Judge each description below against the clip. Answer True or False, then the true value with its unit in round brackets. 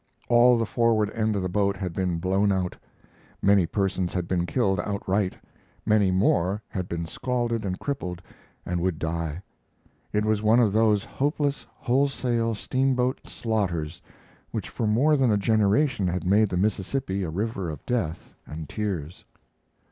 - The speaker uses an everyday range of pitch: True (4.1 semitones)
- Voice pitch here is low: True (100 Hz)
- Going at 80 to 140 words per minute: False (155 wpm)